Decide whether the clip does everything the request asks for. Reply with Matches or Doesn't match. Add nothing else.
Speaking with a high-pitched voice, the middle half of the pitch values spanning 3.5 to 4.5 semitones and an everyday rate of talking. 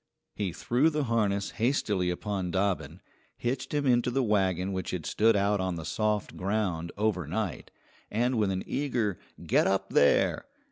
Doesn't match